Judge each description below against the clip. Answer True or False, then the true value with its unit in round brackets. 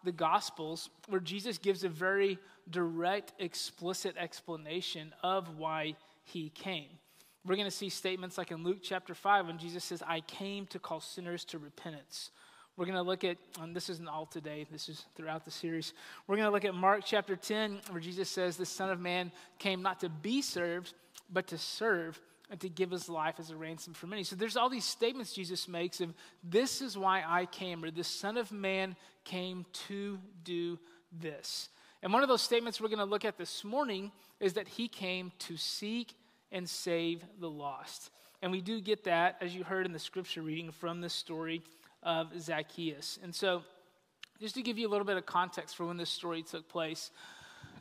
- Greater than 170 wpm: True (205 wpm)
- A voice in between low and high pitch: True (180 Hz)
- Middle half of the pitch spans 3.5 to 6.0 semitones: False (2.7 semitones)